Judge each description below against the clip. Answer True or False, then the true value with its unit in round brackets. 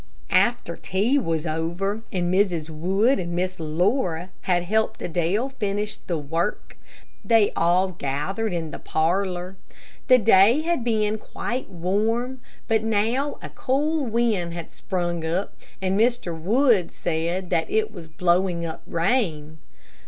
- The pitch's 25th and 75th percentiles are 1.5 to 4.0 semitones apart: False (4.6 semitones)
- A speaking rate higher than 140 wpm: False (135 wpm)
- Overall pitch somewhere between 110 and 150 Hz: False (190 Hz)